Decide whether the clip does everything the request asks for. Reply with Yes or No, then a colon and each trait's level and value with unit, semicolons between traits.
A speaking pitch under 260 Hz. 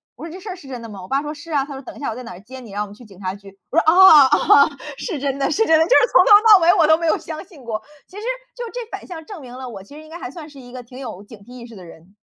No: very high, 275 Hz